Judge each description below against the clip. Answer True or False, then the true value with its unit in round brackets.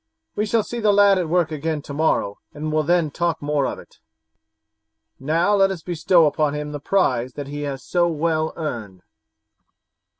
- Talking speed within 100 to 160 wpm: False (175 wpm)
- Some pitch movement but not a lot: True (3.3 semitones)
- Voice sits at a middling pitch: True (155 Hz)